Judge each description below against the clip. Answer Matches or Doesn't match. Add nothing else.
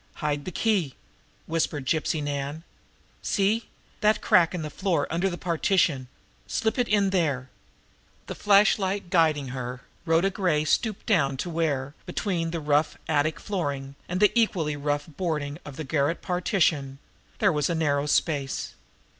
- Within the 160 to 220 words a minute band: Doesn't match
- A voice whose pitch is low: Doesn't match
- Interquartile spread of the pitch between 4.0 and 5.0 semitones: Matches